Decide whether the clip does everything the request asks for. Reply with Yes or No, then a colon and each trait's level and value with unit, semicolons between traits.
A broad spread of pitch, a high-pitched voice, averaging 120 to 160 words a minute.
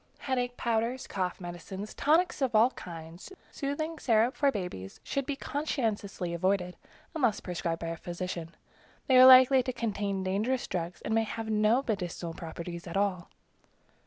Yes: wide, 6.2 semitones; high, 210 Hz; average, 155 wpm